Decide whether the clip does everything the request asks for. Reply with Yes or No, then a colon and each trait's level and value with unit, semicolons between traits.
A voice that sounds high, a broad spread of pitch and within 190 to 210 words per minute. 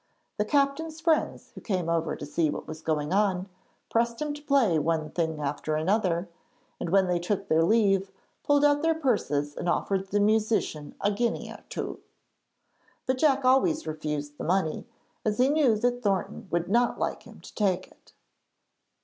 No: high, 200 Hz; wide, 7.2 semitones; average, 175 wpm